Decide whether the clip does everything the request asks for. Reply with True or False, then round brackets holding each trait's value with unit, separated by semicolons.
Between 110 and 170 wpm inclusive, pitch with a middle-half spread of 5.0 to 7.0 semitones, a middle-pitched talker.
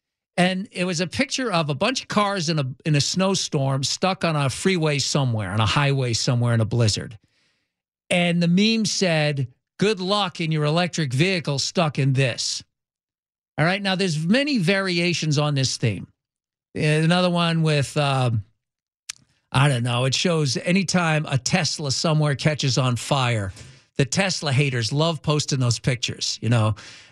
True (165 wpm; 5.4 semitones; 150 Hz)